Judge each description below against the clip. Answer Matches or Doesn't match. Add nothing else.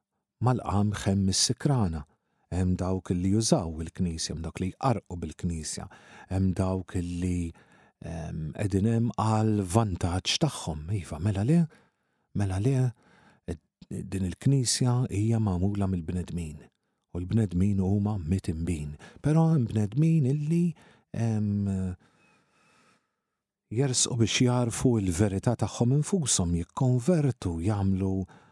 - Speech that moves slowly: Matches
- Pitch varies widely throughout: Doesn't match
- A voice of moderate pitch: Doesn't match